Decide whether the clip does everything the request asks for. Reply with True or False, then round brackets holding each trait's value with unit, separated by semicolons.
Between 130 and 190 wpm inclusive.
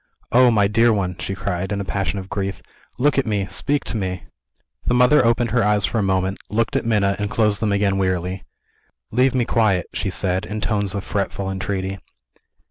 False (205 wpm)